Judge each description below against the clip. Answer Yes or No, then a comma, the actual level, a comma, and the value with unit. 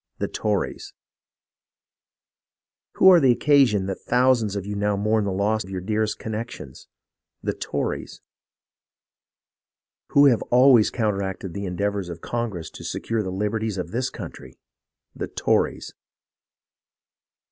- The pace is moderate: No, slow, 125 wpm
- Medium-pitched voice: No, low, 105 Hz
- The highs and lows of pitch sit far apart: No, average, 3.4 semitones